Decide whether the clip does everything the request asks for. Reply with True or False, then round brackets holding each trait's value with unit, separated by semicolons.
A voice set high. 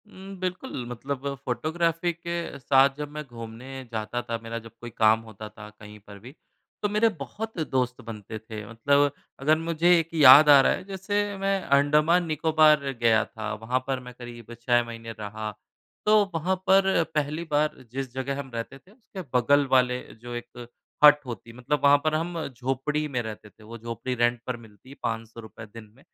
False (135 Hz)